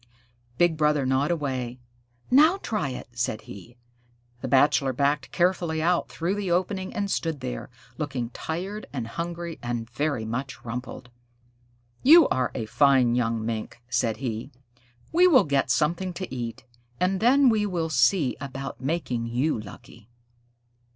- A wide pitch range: Yes, wide, 6.2 semitones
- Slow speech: No, average, 145 wpm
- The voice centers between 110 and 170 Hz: Yes, medium, 140 Hz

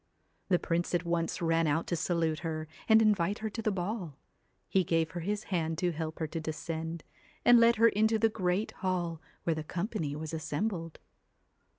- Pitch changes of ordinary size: Yes, average, 4.2 semitones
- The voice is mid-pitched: Yes, medium, 170 Hz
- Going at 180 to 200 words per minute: Yes, average, 190 wpm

